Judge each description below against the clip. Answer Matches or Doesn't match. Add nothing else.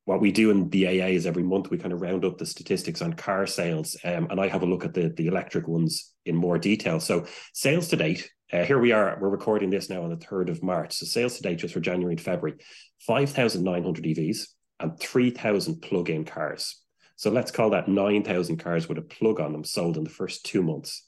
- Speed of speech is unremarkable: Doesn't match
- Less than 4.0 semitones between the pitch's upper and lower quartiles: Matches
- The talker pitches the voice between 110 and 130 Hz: Doesn't match